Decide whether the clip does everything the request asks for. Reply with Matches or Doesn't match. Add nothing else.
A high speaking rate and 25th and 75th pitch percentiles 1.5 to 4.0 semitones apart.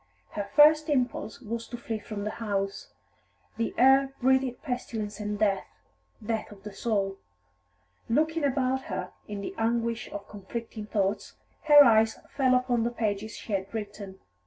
Doesn't match